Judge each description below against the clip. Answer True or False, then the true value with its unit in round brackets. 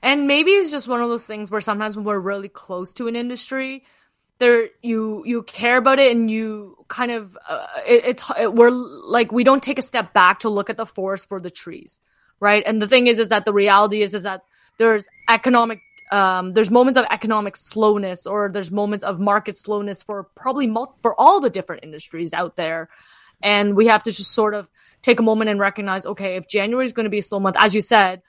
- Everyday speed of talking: False (230 wpm)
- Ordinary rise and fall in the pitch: True (3.1 semitones)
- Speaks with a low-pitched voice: False (215 Hz)